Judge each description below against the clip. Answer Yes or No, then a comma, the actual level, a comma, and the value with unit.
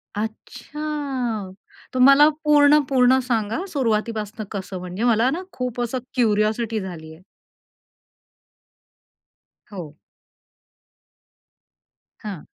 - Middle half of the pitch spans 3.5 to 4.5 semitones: Yes, average, 3.9 semitones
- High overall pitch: Yes, high, 230 Hz